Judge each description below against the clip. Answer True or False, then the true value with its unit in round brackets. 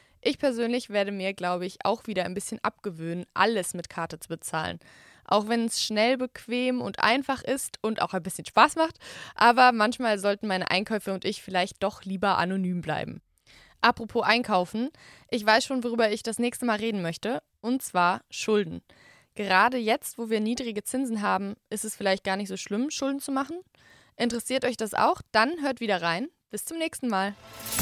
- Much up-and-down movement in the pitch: False (4.1 semitones)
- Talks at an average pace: True (185 wpm)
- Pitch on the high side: True (215 Hz)